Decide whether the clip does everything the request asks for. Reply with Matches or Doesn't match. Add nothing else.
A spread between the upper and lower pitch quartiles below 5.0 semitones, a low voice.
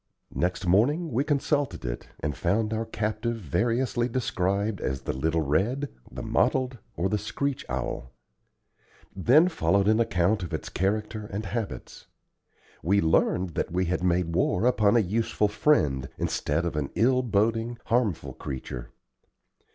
Doesn't match